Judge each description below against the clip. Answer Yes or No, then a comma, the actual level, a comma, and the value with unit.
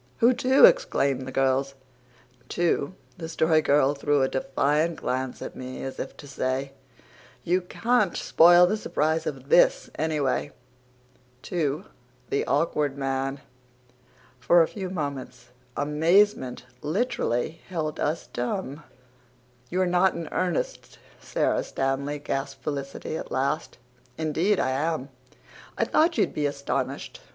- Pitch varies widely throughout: No, average, 4.3 semitones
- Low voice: No, medium, 150 Hz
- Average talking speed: No, slow, 125 wpm